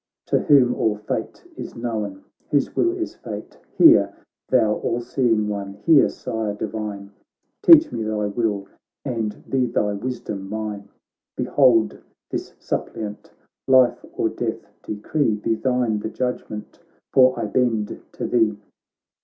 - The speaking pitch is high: No, low, 110 Hz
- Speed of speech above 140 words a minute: No, slow, 135 wpm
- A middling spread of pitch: Yes, average, 3.2 semitones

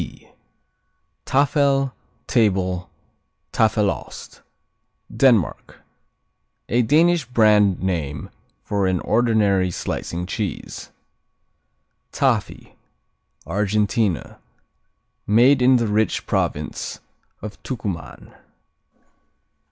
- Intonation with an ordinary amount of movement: Yes, average, 4.6 semitones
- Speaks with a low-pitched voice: Yes, low, 105 Hz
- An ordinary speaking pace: No, slow, 70 wpm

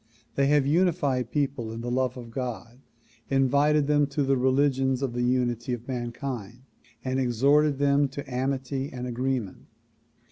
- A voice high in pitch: No, low, 130 Hz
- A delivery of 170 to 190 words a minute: No, average, 150 wpm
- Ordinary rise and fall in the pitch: No, narrow, 2.3 semitones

